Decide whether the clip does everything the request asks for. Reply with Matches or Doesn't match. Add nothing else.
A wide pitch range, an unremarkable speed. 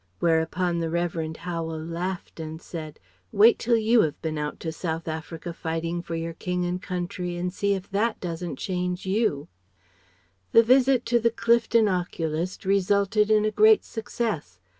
Doesn't match